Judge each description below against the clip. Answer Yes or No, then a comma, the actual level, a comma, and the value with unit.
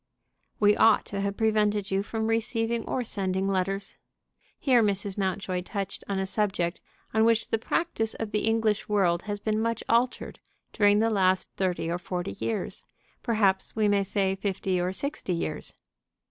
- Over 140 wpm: Yes, average, 165 wpm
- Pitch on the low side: No, high, 205 Hz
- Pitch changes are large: No, average, 2.7 semitones